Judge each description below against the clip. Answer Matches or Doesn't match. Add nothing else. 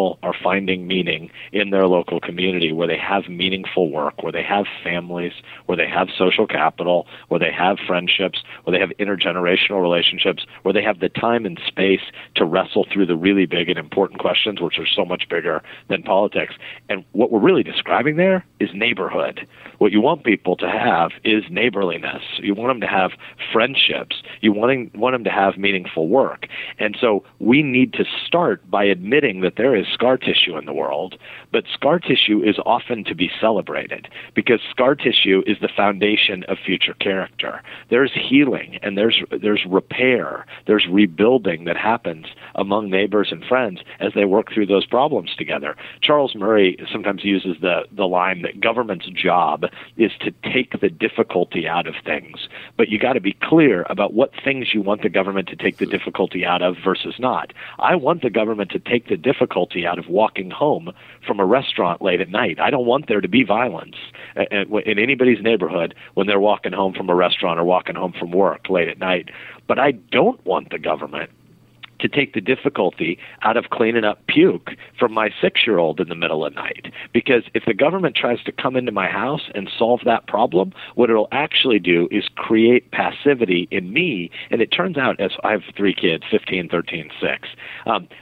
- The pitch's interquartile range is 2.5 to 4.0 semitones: Matches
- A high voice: Doesn't match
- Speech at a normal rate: Matches